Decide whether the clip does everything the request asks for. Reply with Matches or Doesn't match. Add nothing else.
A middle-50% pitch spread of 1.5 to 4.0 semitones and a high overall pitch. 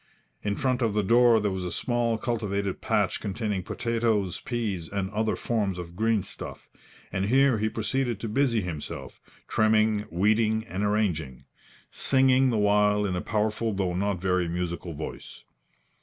Doesn't match